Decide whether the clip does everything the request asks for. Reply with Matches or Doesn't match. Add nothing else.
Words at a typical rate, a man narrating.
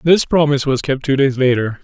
Doesn't match